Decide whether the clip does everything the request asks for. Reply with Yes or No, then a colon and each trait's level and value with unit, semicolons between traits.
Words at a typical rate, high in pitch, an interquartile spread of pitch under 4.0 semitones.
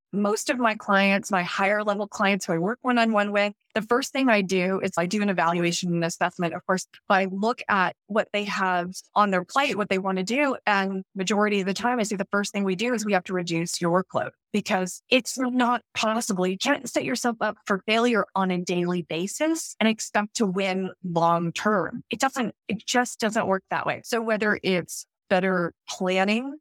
No: fast, 210 wpm; high, 205 Hz; average, 3.3 semitones